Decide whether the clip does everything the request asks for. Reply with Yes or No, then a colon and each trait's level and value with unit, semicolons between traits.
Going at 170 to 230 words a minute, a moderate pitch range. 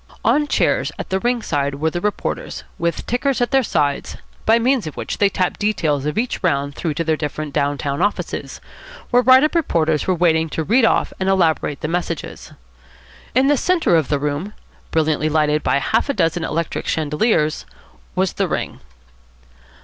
No: average, 180 wpm; wide, 6.7 semitones